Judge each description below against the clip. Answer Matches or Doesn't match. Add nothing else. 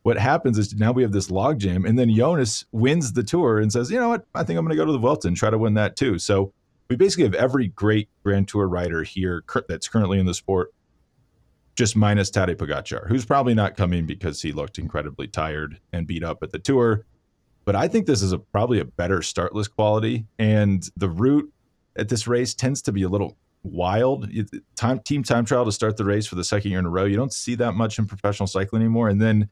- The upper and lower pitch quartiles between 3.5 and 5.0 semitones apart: Matches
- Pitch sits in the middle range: Doesn't match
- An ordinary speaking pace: Doesn't match